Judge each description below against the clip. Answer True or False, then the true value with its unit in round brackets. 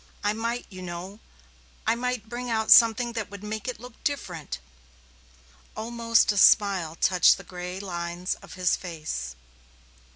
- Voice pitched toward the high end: True (205 Hz)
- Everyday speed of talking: True (150 wpm)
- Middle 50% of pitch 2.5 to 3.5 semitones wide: False (4.4 semitones)